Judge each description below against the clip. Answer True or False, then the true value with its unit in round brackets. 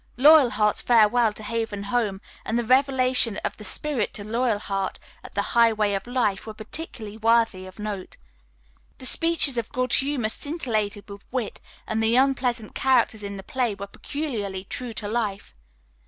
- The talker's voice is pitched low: False (225 Hz)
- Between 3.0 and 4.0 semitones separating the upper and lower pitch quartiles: True (3.6 semitones)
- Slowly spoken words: False (160 wpm)